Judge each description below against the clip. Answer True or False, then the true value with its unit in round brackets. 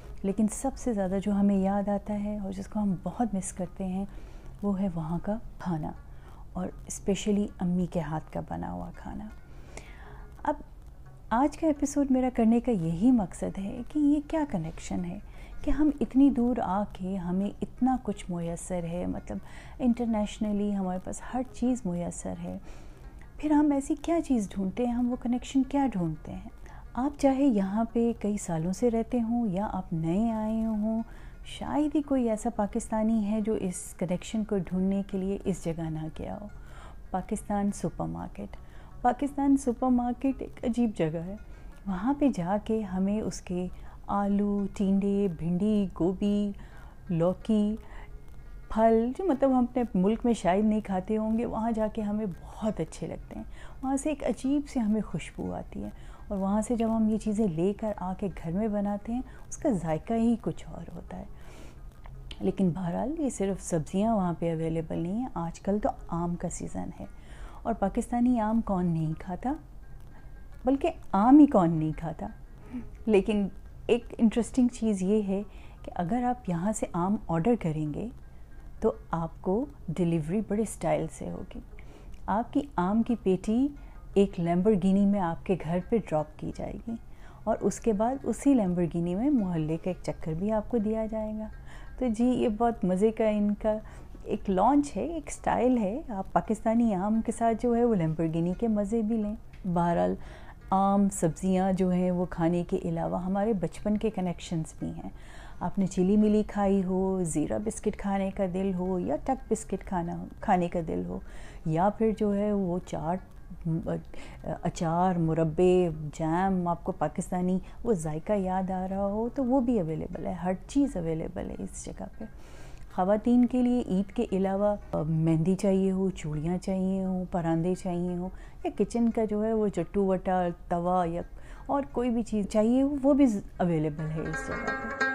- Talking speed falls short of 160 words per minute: False (175 wpm)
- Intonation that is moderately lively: True (4.5 semitones)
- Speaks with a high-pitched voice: True (200 Hz)